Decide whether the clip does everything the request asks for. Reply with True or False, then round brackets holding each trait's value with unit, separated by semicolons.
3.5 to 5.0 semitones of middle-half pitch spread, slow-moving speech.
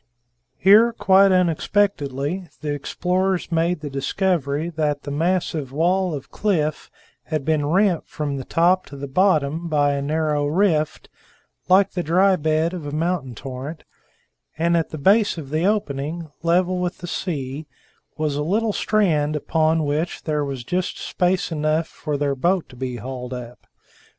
False (4.0 semitones; 160 wpm)